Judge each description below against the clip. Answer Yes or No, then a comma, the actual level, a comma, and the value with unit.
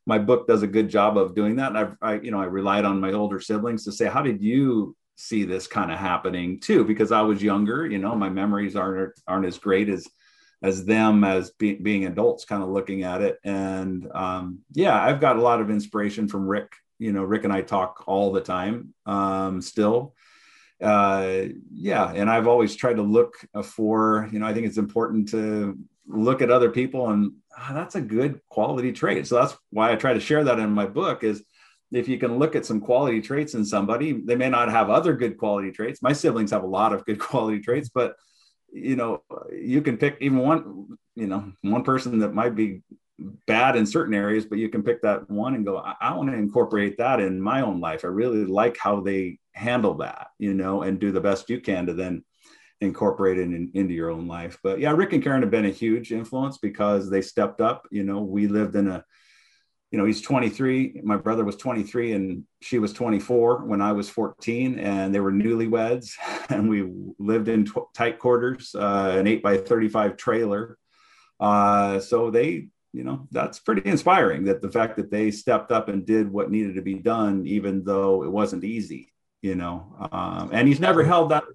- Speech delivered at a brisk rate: Yes, fast, 215 wpm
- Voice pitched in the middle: No, low, 105 Hz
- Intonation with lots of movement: No, average, 2.9 semitones